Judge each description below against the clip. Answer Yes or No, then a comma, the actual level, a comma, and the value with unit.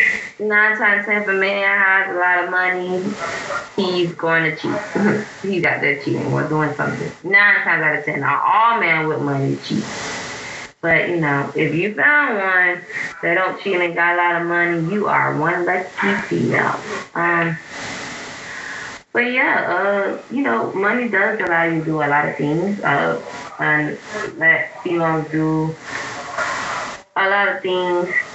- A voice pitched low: No, medium, 175 Hz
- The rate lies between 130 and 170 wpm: Yes, average, 165 wpm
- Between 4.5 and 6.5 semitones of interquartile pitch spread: No, average, 3.6 semitones